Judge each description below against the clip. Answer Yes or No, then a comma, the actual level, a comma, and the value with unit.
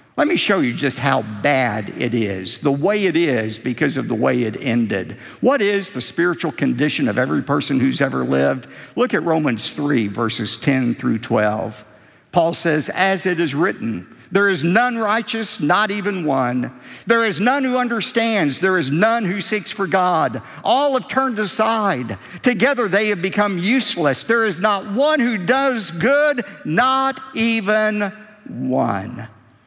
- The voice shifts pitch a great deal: Yes, wide, 8.8 semitones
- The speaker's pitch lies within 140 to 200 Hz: Yes, high, 190 Hz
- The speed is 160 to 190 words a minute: Yes, average, 165 wpm